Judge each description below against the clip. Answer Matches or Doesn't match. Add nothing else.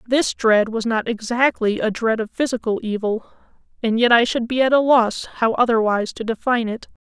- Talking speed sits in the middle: Matches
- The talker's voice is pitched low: Doesn't match